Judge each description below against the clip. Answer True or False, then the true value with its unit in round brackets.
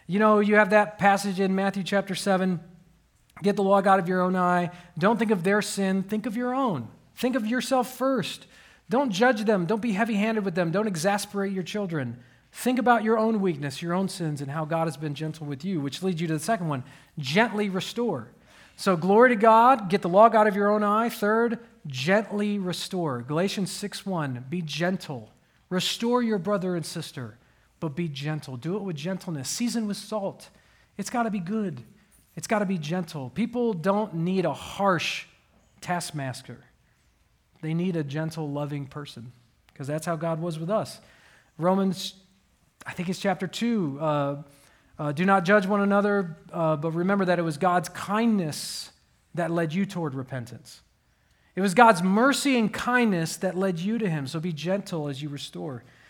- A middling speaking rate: True (185 wpm)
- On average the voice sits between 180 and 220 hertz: True (185 Hz)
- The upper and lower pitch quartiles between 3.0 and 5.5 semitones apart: True (4.7 semitones)